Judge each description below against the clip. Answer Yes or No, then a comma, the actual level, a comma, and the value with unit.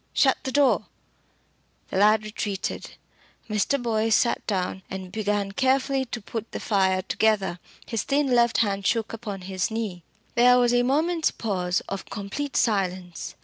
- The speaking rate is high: No, average, 150 wpm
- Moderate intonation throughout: Yes, average, 3.9 semitones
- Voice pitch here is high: Yes, high, 215 Hz